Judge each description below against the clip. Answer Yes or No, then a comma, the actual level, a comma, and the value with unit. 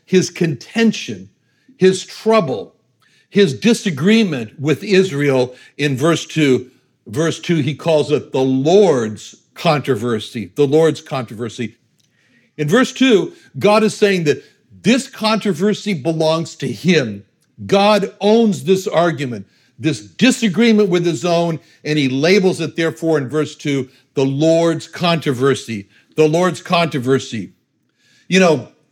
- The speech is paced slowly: Yes, slow, 120 wpm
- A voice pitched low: No, medium, 160 Hz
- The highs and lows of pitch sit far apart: Yes, wide, 5.8 semitones